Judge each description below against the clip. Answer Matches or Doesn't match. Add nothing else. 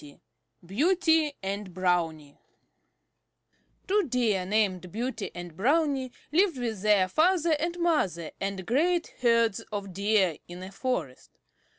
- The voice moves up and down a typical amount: Doesn't match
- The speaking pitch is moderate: Doesn't match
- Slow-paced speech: Matches